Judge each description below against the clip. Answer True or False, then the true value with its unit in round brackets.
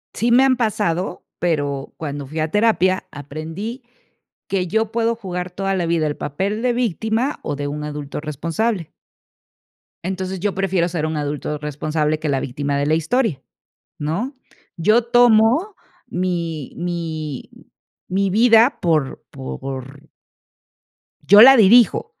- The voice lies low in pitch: False (175 Hz)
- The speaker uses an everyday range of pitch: False (6.6 semitones)